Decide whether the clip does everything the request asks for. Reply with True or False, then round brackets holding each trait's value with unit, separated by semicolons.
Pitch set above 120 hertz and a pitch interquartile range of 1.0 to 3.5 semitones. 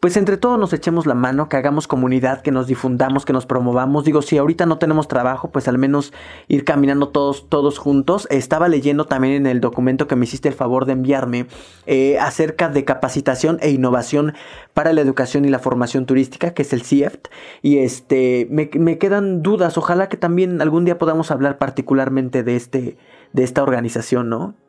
True (140 Hz; 3.2 semitones)